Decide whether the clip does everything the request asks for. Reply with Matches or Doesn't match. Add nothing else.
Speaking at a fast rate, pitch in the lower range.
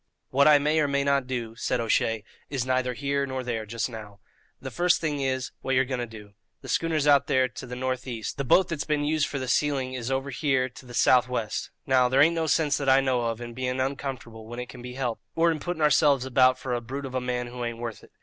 Matches